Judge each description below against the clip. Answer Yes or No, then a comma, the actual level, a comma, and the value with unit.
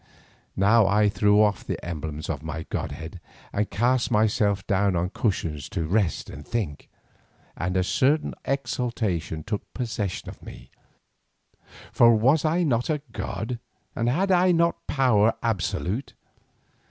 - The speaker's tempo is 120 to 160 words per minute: Yes, average, 140 wpm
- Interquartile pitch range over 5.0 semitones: Yes, wide, 5.5 semitones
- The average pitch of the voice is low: Yes, low, 105 Hz